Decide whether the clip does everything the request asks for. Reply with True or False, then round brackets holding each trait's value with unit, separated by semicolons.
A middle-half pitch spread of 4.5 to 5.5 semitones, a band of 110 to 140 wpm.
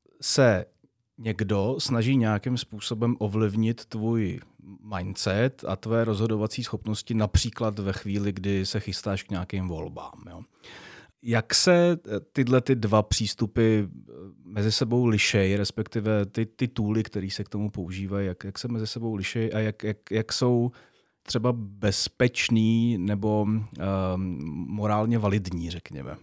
False (2.5 semitones; 135 wpm)